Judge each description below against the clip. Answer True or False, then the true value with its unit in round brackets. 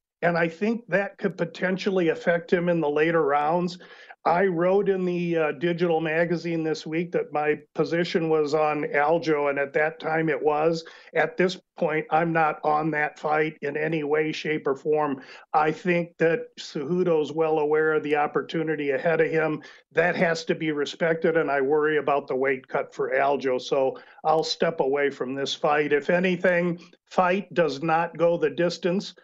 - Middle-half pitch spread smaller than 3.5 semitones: True (2.4 semitones)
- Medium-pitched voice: True (160 Hz)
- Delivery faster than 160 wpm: True (180 wpm)